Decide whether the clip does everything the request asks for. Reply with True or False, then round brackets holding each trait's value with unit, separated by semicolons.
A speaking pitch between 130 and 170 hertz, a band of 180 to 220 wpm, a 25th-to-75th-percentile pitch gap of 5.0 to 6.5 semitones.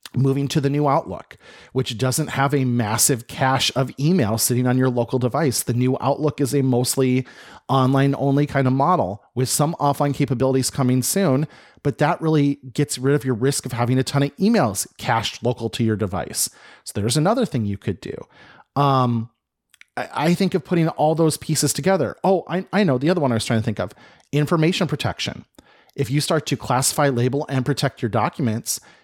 False (135 Hz; 195 wpm; 3.0 semitones)